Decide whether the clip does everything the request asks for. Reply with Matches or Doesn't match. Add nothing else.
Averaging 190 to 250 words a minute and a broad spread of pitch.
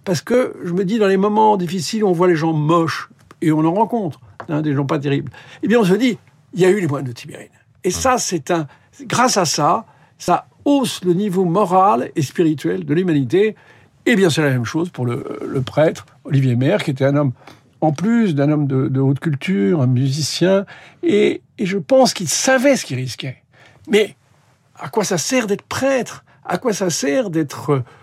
Matches